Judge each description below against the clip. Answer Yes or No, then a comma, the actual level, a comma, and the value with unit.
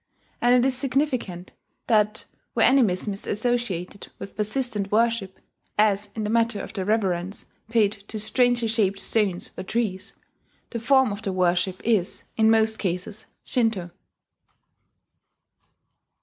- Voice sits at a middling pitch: No, high, 215 Hz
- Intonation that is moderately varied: Yes, average, 3.2 semitones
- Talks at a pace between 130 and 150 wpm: Yes, slow, 135 wpm